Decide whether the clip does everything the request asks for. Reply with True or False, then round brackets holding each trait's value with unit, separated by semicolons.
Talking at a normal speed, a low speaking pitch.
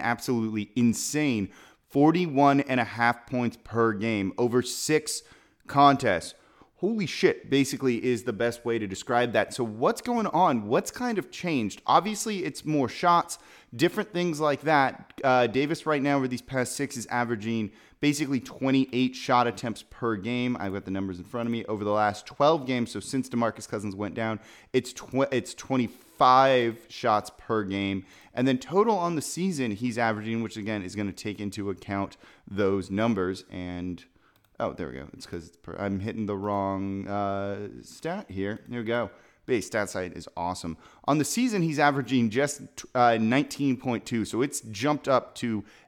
True (175 wpm; 120 Hz)